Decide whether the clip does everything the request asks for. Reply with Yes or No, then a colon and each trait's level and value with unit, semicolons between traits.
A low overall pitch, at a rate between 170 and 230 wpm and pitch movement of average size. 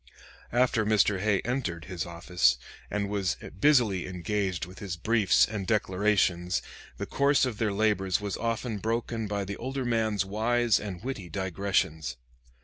No: low, 105 Hz; average, 145 wpm; average, 3.4 semitones